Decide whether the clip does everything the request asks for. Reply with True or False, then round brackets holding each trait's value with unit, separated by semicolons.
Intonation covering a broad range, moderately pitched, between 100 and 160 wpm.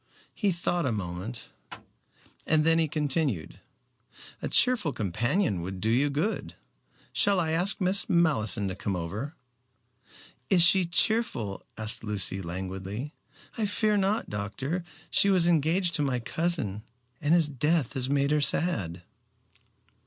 True (8.7 semitones; 145 Hz; 135 wpm)